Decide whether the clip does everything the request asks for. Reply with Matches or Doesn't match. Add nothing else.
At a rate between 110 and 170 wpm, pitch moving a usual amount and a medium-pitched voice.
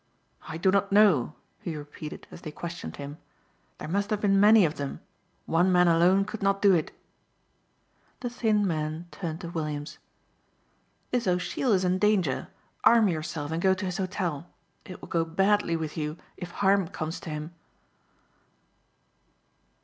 Matches